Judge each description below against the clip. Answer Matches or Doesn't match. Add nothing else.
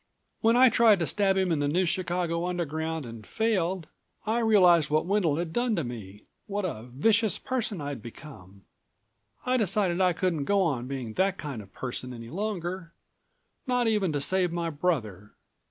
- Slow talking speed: Doesn't match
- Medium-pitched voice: Matches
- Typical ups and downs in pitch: Doesn't match